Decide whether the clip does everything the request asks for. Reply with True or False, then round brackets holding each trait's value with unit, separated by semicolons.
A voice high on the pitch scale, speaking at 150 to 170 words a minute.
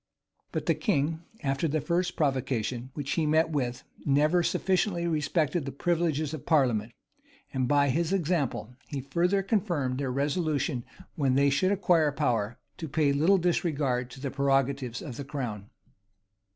False (145 Hz; 155 wpm)